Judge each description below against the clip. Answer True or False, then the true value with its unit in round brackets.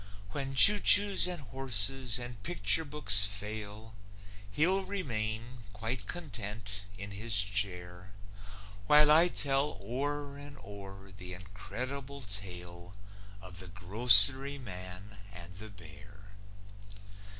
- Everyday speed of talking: False (110 wpm)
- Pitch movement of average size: False (5.7 semitones)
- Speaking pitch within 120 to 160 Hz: False (110 Hz)